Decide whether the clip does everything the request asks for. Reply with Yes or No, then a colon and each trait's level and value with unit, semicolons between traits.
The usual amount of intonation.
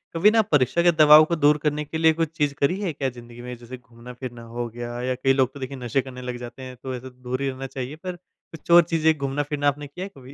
Yes: average, 3.4 semitones